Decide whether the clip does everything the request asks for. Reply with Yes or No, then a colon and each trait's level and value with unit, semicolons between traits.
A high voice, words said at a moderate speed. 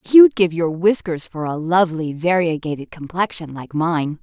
No: medium, 170 Hz; average, 155 wpm